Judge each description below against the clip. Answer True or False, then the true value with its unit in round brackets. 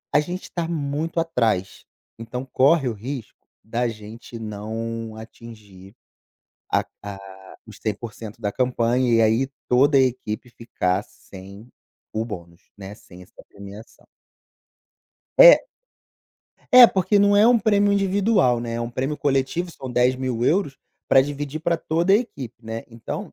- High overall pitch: False (125 Hz)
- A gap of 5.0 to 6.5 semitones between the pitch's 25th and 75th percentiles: True (5.3 semitones)